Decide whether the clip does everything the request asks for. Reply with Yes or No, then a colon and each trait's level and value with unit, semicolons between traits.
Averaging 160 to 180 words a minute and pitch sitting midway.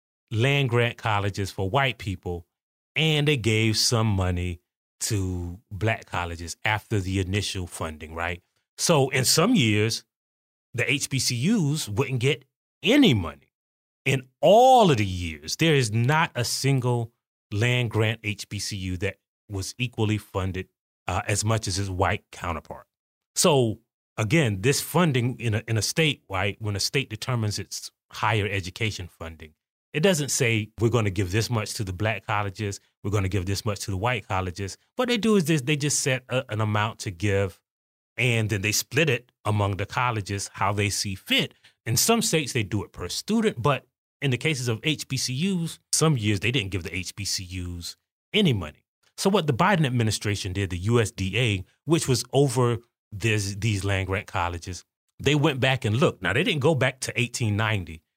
No: average, 175 wpm; low, 110 Hz